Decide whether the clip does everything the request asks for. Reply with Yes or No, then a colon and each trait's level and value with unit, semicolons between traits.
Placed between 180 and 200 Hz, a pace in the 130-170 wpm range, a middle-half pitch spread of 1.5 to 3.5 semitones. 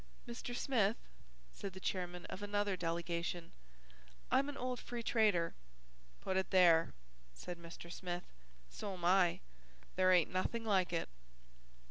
Yes: medium, 185 Hz; slow, 135 wpm; average, 3.1 semitones